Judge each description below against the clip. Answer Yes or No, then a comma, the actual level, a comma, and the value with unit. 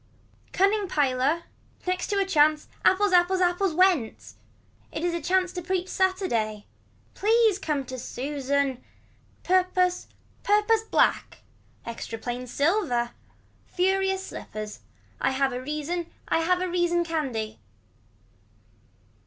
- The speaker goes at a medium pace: No, slow, 110 wpm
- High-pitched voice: Yes, very high, 345 Hz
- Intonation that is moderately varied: No, wide, 5.7 semitones